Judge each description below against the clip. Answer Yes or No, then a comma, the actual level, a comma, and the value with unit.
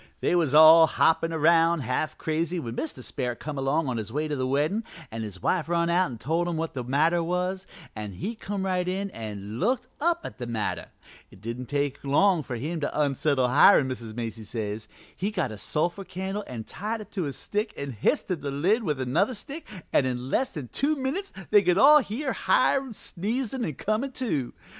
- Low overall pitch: No, medium, 160 Hz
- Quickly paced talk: Yes, fast, 210 wpm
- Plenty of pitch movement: Yes, wide, 7.5 semitones